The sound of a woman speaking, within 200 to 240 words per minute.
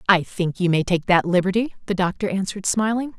Yes: female; fast, 205 wpm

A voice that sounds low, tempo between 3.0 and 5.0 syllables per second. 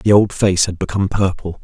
No: very low, 95 Hz; 5.7 syllables/s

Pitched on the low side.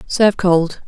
No: medium, 185 Hz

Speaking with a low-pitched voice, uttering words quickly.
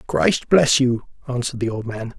No: low, 130 Hz; average, 190 wpm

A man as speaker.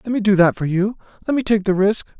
Yes: male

